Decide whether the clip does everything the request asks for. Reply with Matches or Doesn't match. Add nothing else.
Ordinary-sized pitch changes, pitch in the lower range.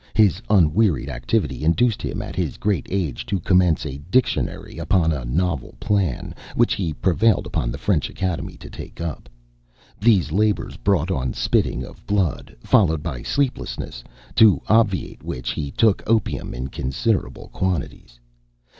Doesn't match